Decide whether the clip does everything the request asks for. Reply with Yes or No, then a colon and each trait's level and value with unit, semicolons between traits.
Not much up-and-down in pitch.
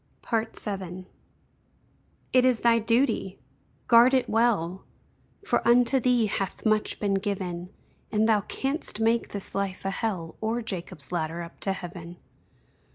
No: average, 3.9 semitones